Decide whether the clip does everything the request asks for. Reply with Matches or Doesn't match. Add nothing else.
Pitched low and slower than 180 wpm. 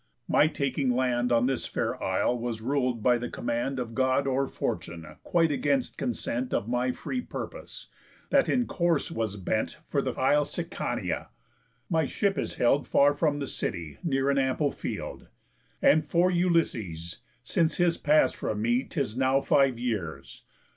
Matches